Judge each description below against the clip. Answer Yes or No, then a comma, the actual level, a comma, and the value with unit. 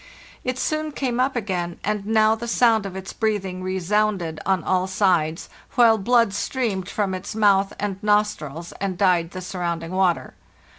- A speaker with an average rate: Yes, average, 160 wpm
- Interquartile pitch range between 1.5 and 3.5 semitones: Yes, average, 3.1 semitones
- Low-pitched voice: No, high, 195 Hz